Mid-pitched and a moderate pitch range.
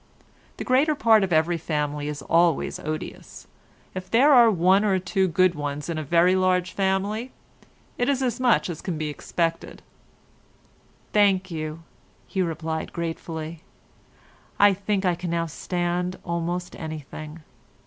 Yes: medium, 175 Hz; average, 3.3 semitones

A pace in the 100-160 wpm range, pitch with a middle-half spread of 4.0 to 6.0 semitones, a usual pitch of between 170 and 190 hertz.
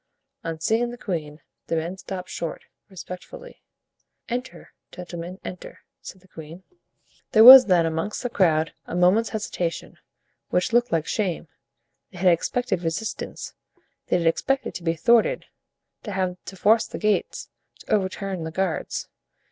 Yes: average, 150 wpm; average, 4.6 semitones; medium, 185 Hz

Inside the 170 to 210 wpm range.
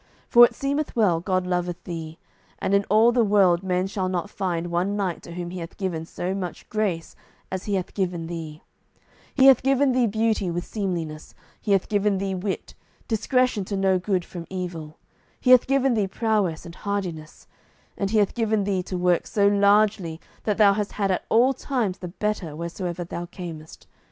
Yes: average, 190 wpm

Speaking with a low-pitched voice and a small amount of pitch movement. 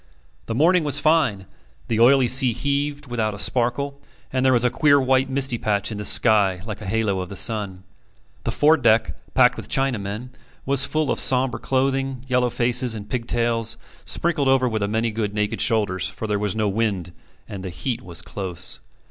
No: low, 120 Hz; average, 4.2 semitones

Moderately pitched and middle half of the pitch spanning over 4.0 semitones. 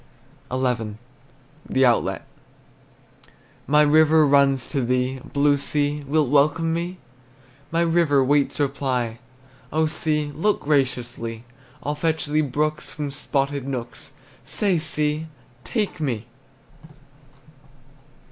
No: medium, 145 Hz; average, 2.8 semitones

